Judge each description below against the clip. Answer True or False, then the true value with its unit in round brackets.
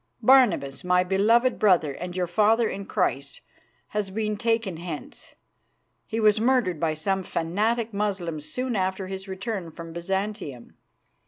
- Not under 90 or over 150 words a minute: True (140 wpm)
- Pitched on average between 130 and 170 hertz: False (195 Hz)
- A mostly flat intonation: False (3.9 semitones)